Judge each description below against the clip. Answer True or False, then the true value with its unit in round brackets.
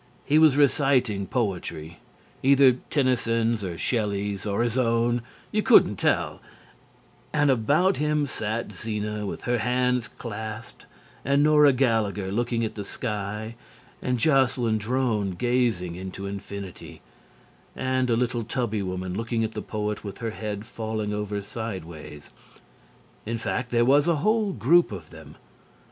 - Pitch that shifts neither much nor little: True (3.8 semitones)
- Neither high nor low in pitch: False (115 Hz)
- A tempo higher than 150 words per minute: False (140 wpm)